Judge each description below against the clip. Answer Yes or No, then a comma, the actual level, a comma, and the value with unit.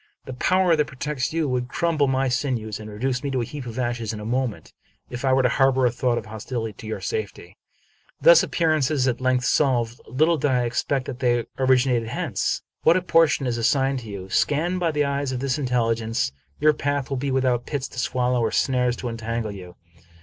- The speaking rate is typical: No, fast, 220 wpm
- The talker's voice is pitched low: Yes, low, 130 Hz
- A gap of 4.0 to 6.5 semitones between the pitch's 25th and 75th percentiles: No, average, 3.1 semitones